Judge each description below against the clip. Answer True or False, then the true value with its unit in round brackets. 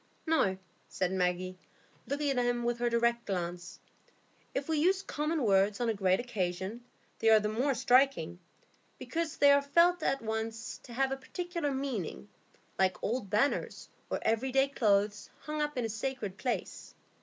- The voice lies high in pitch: True (240 Hz)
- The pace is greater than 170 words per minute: False (165 wpm)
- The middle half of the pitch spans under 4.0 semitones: False (5.6 semitones)